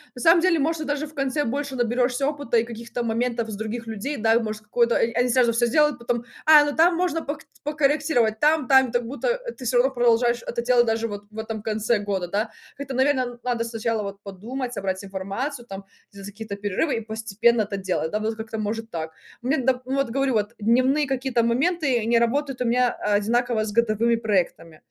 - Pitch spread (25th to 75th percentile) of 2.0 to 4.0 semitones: Yes, average, 3.5 semitones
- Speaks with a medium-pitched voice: No, high, 235 Hz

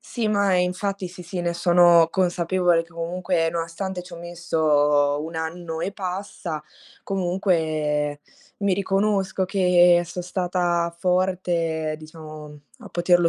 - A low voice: No, medium, 175 Hz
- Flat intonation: Yes, narrow, 2.1 semitones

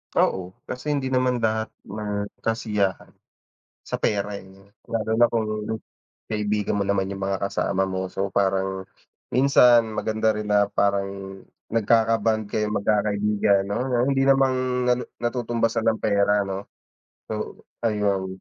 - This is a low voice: Yes, low, 105 Hz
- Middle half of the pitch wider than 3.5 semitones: No, narrow, 2.4 semitones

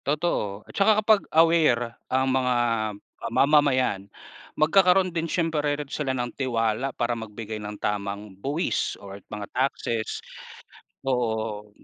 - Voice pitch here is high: No, low, 125 Hz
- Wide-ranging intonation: Yes, wide, 6.1 semitones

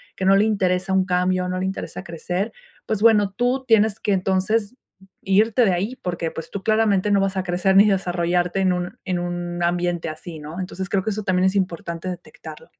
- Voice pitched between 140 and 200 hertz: Yes, high, 190 Hz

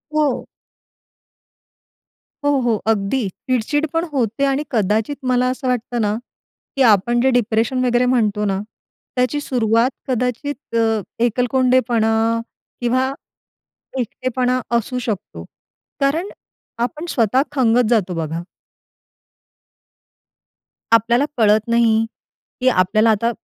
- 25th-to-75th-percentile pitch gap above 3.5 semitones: No, average, 2.8 semitones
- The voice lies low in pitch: No, high, 240 Hz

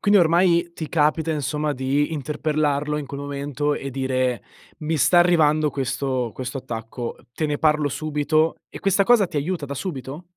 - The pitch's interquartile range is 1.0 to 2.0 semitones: No, narrow, 2.6 semitones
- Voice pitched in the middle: Yes, medium, 150 Hz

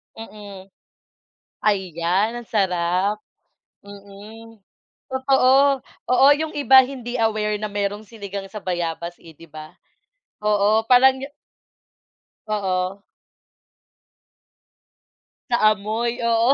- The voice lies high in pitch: Yes, high, 210 Hz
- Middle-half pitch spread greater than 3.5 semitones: No, average, 3.2 semitones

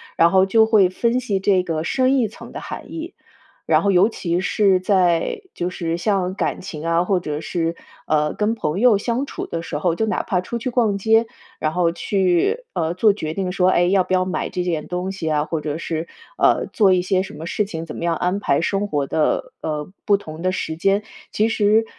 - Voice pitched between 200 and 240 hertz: No, medium, 185 Hz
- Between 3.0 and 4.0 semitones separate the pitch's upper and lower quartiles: Yes, average, 3.7 semitones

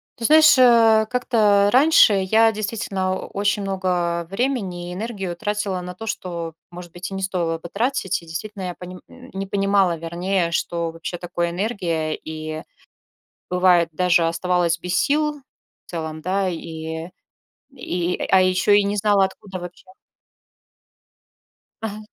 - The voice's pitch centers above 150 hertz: Yes, medium, 185 Hz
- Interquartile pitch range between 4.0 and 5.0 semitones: No, average, 3.2 semitones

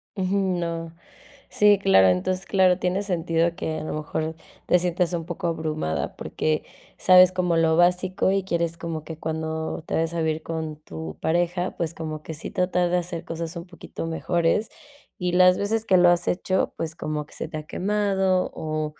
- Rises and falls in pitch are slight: Yes, narrow, 2.3 semitones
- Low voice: No, medium, 170 Hz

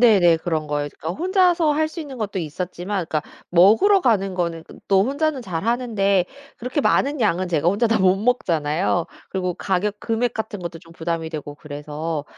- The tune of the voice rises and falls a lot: Yes, wide, 6.1 semitones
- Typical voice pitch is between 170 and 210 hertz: Yes, high, 190 Hz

